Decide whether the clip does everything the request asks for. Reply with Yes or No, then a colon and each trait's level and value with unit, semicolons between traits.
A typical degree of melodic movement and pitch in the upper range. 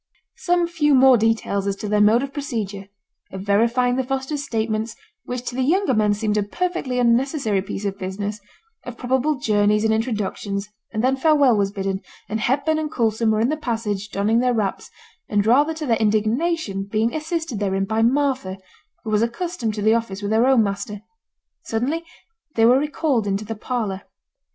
Yes: average, 4.3 semitones; high, 225 Hz